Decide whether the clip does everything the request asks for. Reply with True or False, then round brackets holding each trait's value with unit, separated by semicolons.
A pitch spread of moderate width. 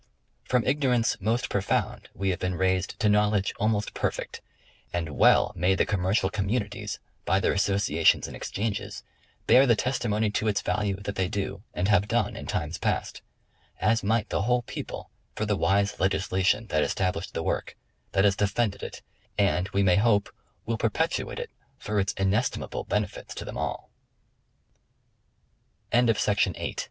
False (2.0 semitones)